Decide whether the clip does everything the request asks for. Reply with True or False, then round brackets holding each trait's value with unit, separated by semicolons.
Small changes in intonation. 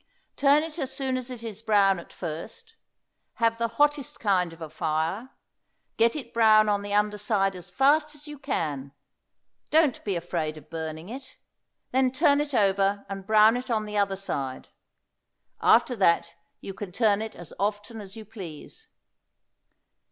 False (5.3 semitones)